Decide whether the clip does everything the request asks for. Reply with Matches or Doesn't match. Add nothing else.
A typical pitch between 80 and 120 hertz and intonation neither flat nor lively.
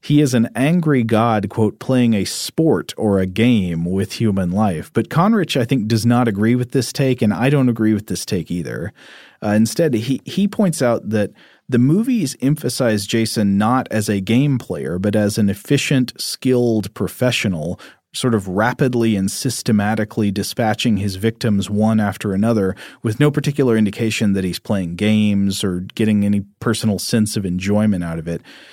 Matches